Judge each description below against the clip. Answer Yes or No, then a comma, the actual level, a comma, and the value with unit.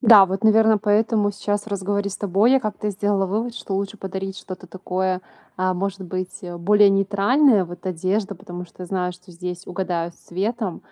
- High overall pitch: Yes, high, 195 Hz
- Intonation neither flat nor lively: No, narrow, 2.1 semitones